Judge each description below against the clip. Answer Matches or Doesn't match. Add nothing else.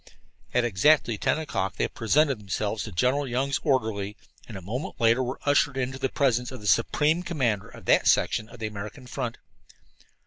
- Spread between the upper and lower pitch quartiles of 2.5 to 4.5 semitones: Matches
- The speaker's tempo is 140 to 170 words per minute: Doesn't match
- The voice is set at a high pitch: Doesn't match